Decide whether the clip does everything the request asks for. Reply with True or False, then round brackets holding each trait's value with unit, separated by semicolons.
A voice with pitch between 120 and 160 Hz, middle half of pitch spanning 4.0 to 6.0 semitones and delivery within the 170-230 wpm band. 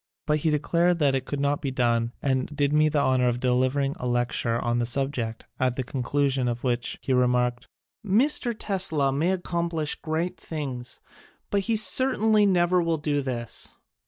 True (140 Hz; 5.1 semitones; 180 wpm)